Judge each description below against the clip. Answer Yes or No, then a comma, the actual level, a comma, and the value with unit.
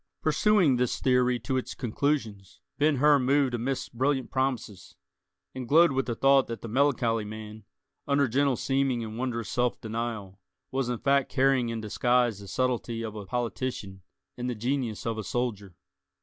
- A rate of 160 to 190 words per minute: Yes, average, 165 wpm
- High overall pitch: No, low, 125 Hz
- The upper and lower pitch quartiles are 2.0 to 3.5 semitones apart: Yes, average, 3.2 semitones